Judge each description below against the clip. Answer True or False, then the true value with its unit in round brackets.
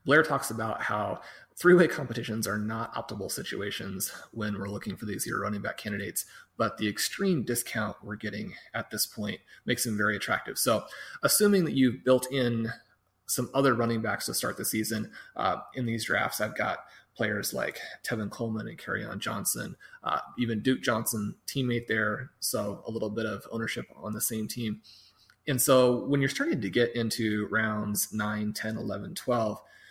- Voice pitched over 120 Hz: False (115 Hz)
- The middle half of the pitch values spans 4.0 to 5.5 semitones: False (2.8 semitones)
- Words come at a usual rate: True (180 wpm)